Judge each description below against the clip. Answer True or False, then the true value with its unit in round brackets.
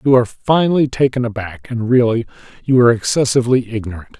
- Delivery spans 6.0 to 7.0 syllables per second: True (6.5 syllables/s)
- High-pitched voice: False (120 Hz)